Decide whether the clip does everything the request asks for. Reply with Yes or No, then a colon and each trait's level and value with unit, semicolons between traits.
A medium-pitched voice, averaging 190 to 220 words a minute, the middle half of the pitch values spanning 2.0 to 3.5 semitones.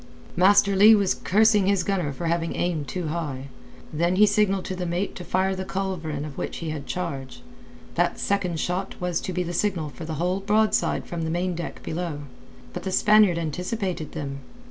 Yes: medium, 180 Hz; average, 195 wpm; average, 3.1 semitones